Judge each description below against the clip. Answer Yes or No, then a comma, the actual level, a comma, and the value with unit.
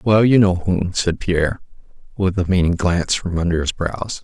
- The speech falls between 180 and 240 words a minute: Yes, average, 200 wpm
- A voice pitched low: Yes, very low, 90 Hz